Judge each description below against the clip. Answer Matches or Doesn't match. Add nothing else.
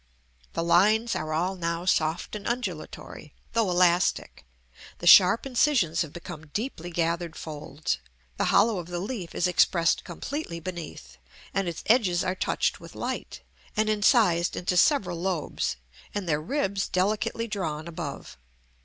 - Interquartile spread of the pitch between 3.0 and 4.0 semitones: Matches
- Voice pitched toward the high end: Doesn't match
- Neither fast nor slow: Matches